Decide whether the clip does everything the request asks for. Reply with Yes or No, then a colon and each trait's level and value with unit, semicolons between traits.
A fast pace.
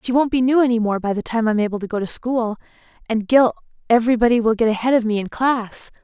Yes: fast, 240 wpm